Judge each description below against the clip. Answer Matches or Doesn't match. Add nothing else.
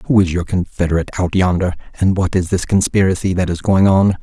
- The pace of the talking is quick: Matches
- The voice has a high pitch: Doesn't match